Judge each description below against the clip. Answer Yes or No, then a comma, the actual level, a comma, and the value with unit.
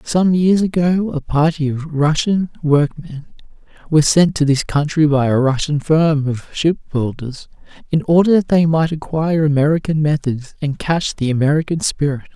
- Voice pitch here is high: No, medium, 155 Hz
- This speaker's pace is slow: No, average, 155 wpm